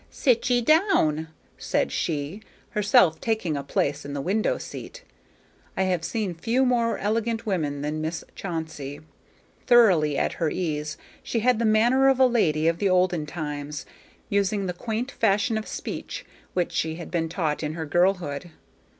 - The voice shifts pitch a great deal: Yes, wide, 6.3 semitones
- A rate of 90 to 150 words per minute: No, average, 165 wpm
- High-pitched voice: No, medium, 180 Hz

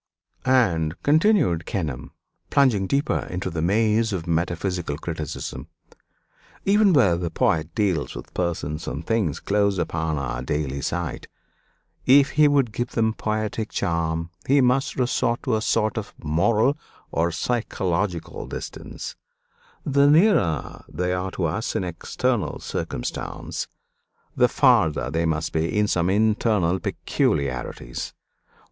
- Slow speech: Yes, slow, 125 wpm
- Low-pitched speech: Yes, very low, 95 Hz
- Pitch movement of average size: No, wide, 6.2 semitones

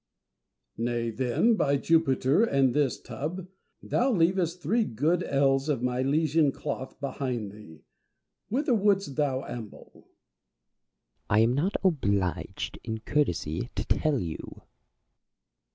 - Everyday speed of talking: No, slow, 120 wpm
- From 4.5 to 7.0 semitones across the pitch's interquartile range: Yes, wide, 5.5 semitones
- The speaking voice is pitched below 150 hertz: Yes, medium, 140 Hz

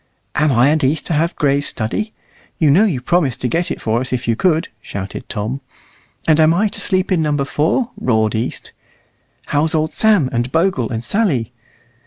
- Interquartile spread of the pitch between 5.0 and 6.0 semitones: Yes, wide, 5.6 semitones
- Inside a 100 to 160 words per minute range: No, average, 195 wpm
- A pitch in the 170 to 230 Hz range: No, medium, 150 Hz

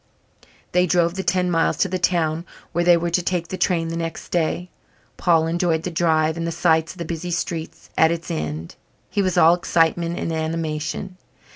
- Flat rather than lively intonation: Yes, narrow, 1.6 semitones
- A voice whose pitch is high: No, medium, 170 Hz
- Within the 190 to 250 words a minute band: Yes, average, 195 wpm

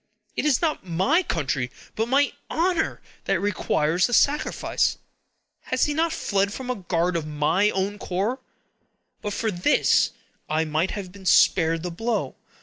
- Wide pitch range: Yes, wide, 7.0 semitones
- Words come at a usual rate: Yes, average, 155 wpm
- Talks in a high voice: Yes, high, 195 Hz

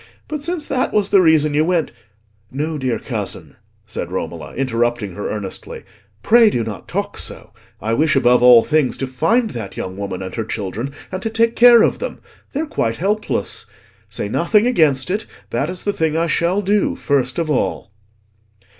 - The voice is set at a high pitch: No, medium, 155 Hz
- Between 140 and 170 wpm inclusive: No, average, 185 wpm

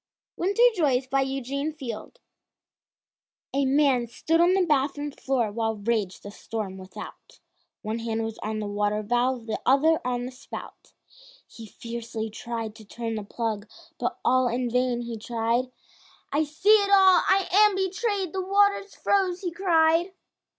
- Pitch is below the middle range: No, very high, 255 Hz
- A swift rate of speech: No, average, 155 wpm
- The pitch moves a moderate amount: No, wide, 7.1 semitones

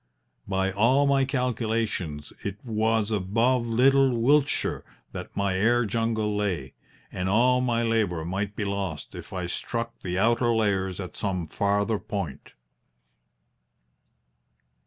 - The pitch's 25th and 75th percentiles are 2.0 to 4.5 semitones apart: Yes, average, 3.6 semitones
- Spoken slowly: Yes, slow, 125 wpm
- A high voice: No, low, 110 Hz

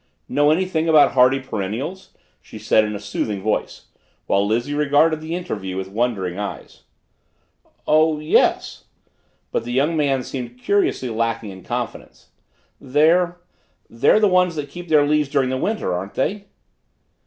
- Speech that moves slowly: No, average, 150 wpm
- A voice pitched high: No, low, 135 Hz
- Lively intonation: Yes, wide, 6.3 semitones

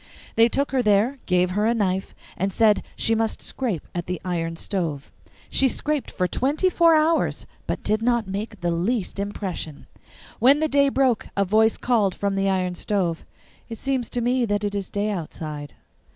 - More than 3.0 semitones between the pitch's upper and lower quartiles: Yes, average, 5.2 semitones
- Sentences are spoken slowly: No, average, 185 wpm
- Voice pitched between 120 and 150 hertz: No, high, 210 Hz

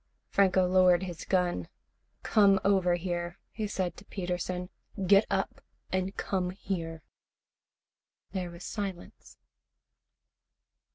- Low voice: No, medium, 185 Hz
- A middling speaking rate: No, slow, 105 wpm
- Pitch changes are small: Yes, narrow, 1.7 semitones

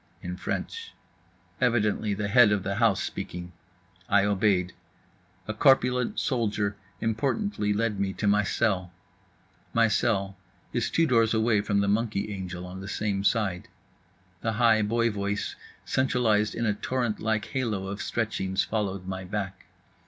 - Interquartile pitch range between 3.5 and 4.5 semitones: No, average, 2.7 semitones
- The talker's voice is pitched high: No, low, 105 Hz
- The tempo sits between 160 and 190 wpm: No, average, 145 wpm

